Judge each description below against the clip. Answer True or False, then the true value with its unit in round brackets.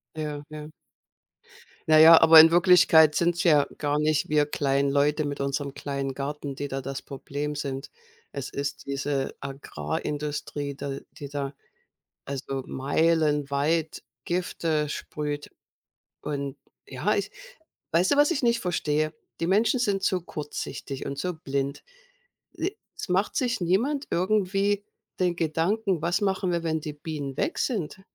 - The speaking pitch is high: False (150 Hz)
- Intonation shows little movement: False (3.8 semitones)